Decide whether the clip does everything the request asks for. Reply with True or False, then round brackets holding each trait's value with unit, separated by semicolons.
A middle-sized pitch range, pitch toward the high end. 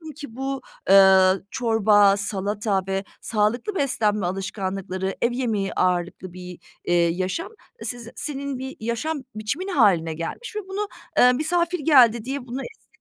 False (6.0 semitones; 220 Hz)